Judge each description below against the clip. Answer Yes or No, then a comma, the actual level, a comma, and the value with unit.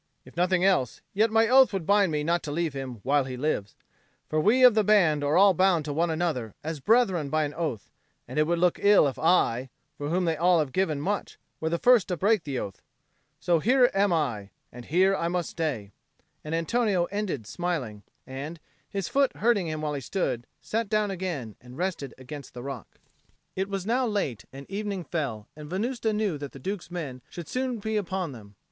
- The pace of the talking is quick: Yes, fast, 210 wpm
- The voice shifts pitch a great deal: Yes, wide, 5.8 semitones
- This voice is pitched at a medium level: Yes, medium, 170 Hz